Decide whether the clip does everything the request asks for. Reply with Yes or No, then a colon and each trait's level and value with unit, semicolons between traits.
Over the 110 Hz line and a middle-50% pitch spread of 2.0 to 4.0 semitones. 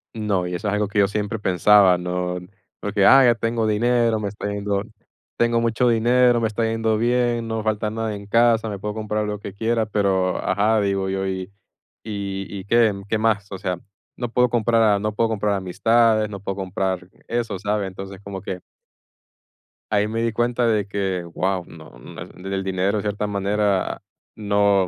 No: low, 105 Hz; narrow, 2.5 semitones